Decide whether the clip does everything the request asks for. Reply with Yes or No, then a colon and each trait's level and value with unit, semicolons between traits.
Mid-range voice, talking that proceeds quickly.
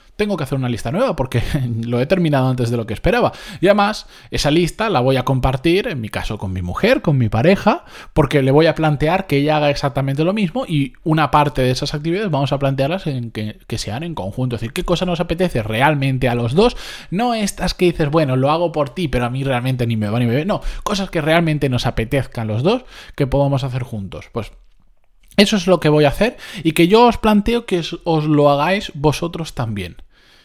Yes: medium, 150 Hz; fast, 235 wpm